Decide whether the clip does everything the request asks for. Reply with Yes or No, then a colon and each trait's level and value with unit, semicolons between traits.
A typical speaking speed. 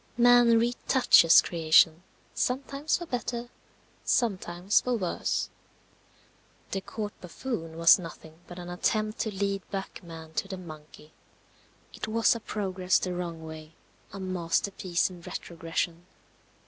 No: slow, 125 wpm